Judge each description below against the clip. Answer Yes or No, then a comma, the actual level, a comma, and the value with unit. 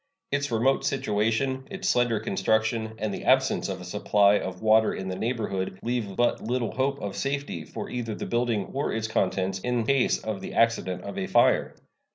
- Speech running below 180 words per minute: No, average, 190 wpm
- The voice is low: Yes, low, 110 Hz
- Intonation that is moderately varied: Yes, average, 3.7 semitones